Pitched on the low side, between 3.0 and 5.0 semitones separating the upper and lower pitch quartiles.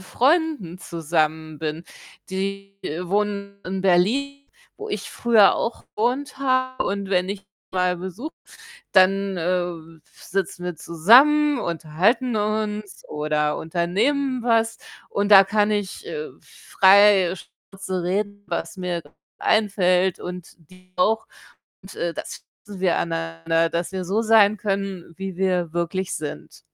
No: high, 195 Hz; average, 3.5 semitones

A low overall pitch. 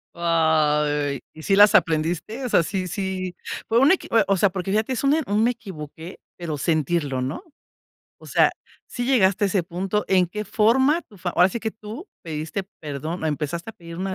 No: medium, 185 Hz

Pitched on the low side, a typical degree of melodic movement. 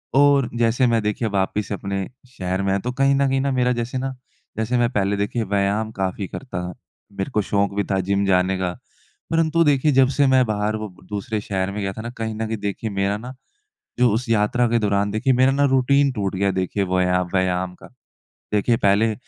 Yes: low, 105 Hz; average, 4.2 semitones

